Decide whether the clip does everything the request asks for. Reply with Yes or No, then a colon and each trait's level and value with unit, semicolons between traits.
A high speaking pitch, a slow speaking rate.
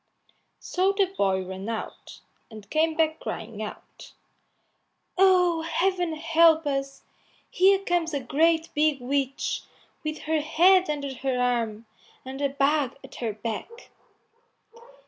Yes: very high, 300 Hz; slow, 125 wpm